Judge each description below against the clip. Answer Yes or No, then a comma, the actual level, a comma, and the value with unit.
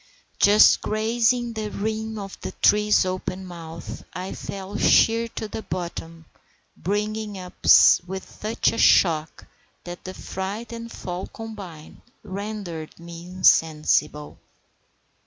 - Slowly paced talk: Yes, slow, 120 wpm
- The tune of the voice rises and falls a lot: No, average, 3.8 semitones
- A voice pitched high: Yes, high, 195 Hz